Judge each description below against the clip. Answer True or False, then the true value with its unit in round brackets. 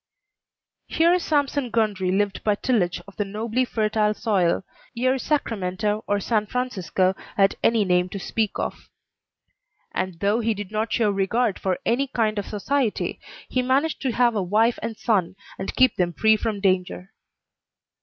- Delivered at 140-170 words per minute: True (160 wpm)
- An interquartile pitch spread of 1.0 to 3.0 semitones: False (3.5 semitones)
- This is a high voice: True (215 Hz)